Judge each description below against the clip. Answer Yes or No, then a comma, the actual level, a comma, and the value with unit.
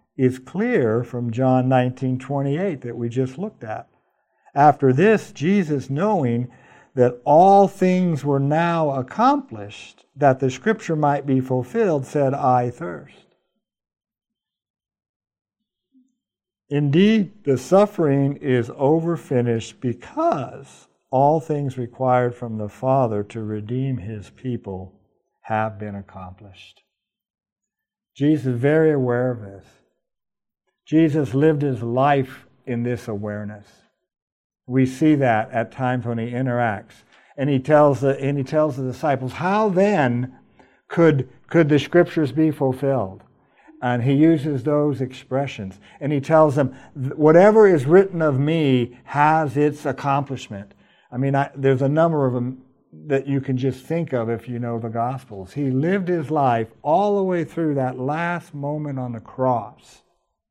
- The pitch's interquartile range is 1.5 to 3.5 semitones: No, average, 4.0 semitones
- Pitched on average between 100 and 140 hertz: Yes, low, 135 Hz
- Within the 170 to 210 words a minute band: No, slow, 135 wpm